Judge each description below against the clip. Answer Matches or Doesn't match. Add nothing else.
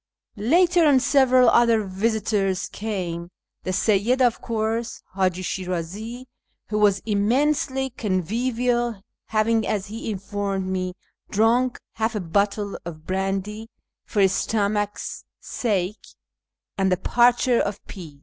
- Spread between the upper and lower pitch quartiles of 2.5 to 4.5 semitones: Matches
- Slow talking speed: Matches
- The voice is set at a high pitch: Matches